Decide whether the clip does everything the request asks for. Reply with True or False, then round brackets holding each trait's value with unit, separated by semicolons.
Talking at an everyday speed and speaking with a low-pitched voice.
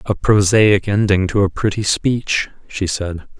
True (160 wpm; 100 Hz)